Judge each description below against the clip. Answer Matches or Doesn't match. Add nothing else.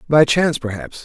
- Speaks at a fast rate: Doesn't match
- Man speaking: Matches